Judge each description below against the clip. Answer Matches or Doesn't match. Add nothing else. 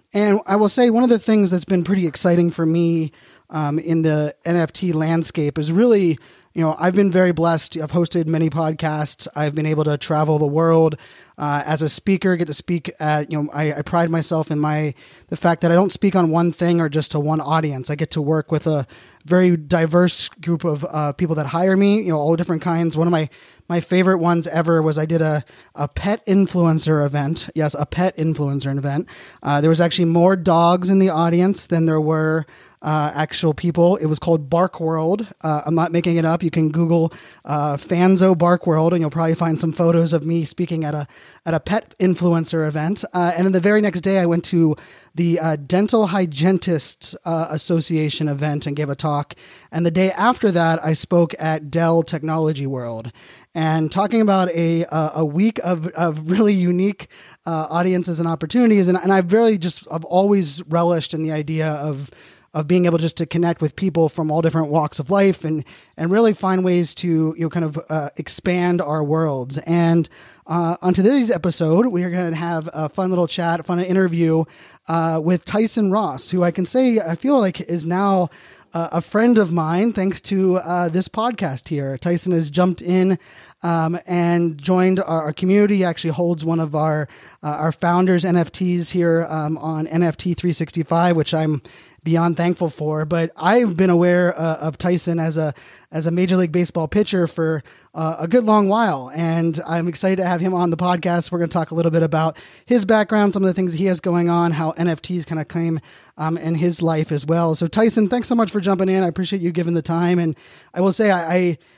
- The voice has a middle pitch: Matches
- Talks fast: Matches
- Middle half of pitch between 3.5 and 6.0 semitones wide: Doesn't match